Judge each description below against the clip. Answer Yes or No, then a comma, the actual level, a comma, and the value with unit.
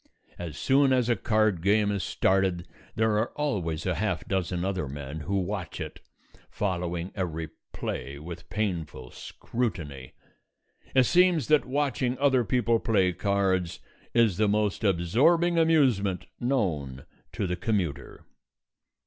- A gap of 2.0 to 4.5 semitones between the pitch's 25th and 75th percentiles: No, wide, 5.5 semitones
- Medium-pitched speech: No, low, 100 Hz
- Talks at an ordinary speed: No, slow, 130 wpm